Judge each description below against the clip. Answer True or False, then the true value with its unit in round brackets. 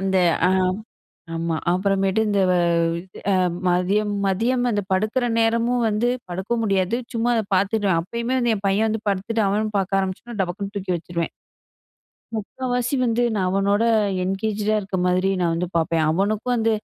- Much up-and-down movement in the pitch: False (3.3 semitones)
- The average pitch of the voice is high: True (200 Hz)